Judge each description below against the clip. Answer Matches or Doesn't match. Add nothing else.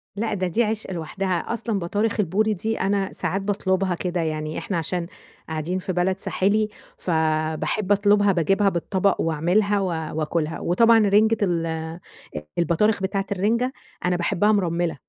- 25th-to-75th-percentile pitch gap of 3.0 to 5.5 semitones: Matches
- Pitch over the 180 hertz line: Matches